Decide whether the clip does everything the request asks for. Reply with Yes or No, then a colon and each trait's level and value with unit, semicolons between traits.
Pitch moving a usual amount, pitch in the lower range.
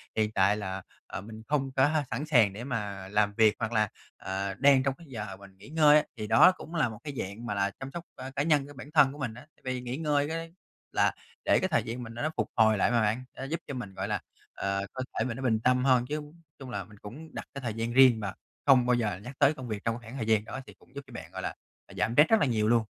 Yes: average, 4.6 semitones; low, 120 Hz